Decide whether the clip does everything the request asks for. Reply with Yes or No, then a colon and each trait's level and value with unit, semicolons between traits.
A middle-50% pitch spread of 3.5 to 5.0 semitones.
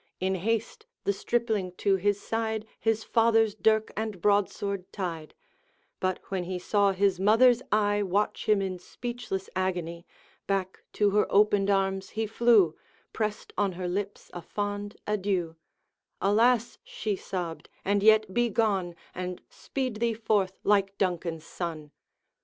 No: average, 2.7 semitones